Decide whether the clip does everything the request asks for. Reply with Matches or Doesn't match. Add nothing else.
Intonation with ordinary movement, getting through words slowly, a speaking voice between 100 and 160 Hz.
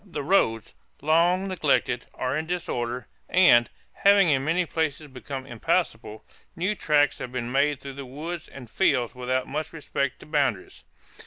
Doesn't match